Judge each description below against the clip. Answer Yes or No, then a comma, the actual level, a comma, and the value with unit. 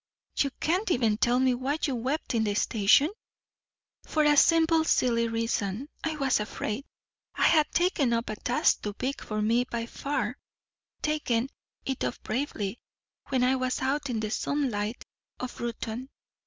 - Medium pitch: No, very high, 250 Hz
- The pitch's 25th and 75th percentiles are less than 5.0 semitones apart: Yes, average, 3.9 semitones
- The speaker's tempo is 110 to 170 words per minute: Yes, average, 160 wpm